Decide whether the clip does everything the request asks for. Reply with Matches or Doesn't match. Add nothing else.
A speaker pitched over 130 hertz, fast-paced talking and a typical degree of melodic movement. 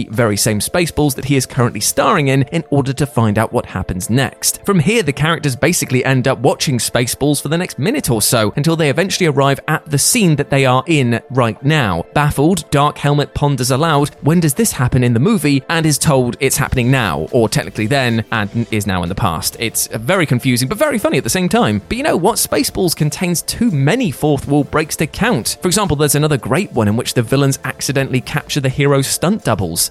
Matches